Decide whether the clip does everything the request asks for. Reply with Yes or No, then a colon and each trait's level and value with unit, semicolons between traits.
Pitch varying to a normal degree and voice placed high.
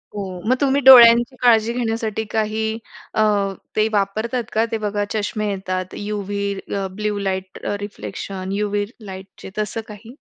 No: narrow, 2.1 semitones; high, 210 Hz